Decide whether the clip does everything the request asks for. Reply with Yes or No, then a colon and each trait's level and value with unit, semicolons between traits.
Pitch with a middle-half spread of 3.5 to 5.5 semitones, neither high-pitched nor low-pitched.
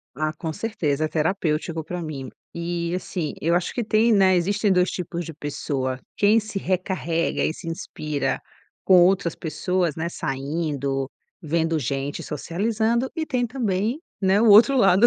Yes: average, 4.6 semitones; medium, 175 Hz